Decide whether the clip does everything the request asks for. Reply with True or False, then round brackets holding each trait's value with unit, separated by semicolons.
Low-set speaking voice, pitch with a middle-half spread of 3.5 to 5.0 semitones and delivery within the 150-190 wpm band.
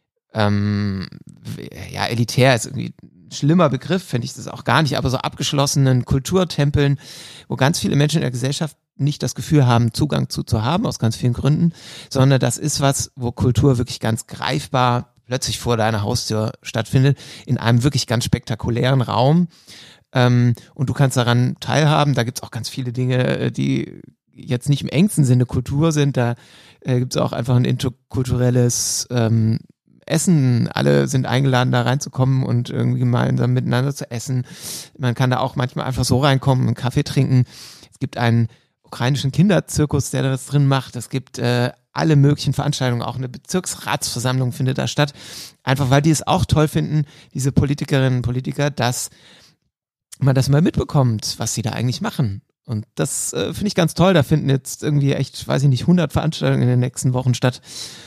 False (130 Hz; 3.0 semitones; 180 wpm)